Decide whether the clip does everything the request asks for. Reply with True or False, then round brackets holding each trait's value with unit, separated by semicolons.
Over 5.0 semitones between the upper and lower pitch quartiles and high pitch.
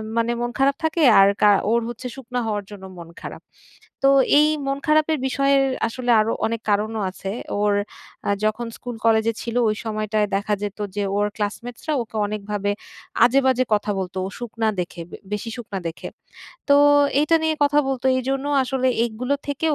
False (4.1 semitones; 230 Hz)